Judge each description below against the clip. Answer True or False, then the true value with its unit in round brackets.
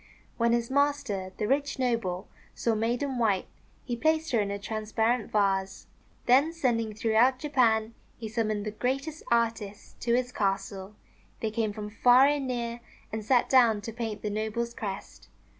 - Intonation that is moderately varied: True (3.0 semitones)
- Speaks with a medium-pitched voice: False (230 Hz)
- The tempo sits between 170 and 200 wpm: False (160 wpm)